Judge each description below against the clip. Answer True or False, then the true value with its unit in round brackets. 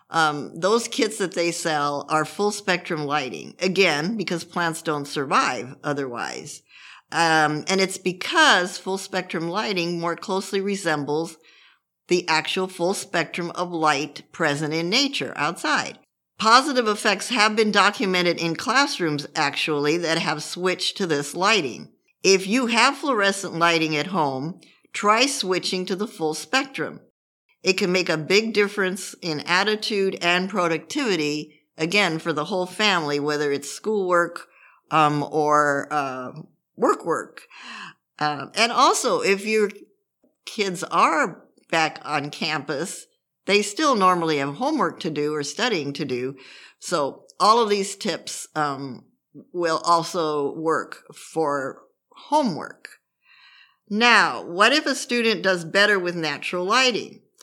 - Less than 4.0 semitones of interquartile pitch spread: False (4.8 semitones)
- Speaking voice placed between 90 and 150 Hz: False (175 Hz)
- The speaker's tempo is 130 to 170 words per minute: True (135 wpm)